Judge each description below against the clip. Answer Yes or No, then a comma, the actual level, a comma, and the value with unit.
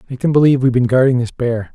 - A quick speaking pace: Yes, fast, 275 wpm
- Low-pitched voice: Yes, low, 125 Hz